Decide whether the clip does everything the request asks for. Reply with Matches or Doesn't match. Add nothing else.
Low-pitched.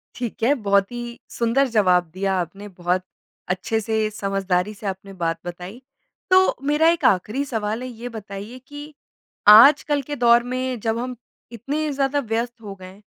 Doesn't match